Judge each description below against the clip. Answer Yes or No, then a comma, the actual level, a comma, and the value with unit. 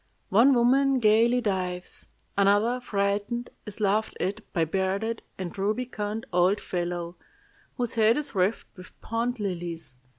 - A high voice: Yes, high, 205 Hz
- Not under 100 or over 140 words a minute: Yes, slow, 135 wpm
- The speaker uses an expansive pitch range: No, average, 4.0 semitones